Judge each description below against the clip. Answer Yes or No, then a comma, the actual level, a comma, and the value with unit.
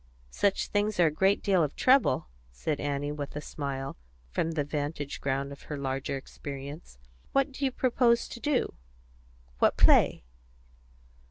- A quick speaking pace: No, average, 155 wpm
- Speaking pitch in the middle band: Yes, medium, 150 Hz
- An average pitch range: No, wide, 6.7 semitones